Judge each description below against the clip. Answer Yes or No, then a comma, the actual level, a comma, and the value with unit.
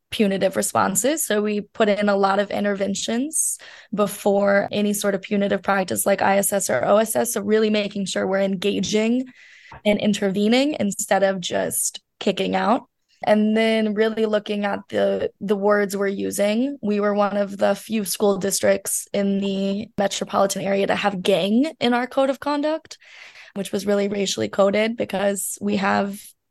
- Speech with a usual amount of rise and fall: No, narrow, 1.5 semitones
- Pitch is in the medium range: No, high, 205 Hz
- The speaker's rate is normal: Yes, average, 160 wpm